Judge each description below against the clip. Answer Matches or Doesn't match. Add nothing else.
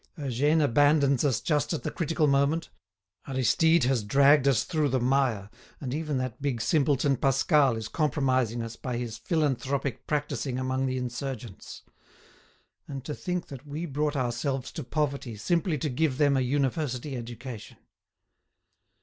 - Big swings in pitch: Doesn't match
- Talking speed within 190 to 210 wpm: Doesn't match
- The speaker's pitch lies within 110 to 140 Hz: Matches